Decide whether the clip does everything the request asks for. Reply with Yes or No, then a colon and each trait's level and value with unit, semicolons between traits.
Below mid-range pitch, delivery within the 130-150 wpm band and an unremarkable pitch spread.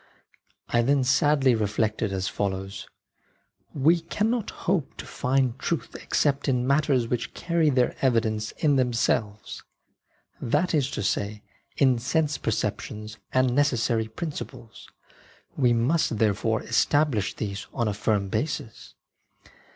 Yes: low, 125 Hz; average, 140 wpm; average, 4.7 semitones